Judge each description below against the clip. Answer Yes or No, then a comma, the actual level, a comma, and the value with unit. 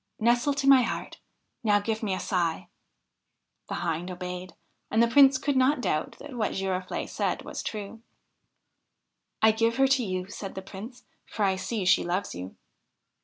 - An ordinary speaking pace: Yes, average, 190 wpm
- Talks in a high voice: Yes, high, 210 Hz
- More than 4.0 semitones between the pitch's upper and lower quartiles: Yes, average, 4.7 semitones